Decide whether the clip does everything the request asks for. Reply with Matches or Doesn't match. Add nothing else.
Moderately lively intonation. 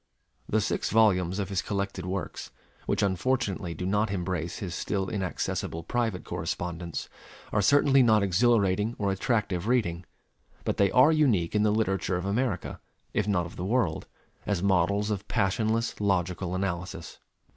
Matches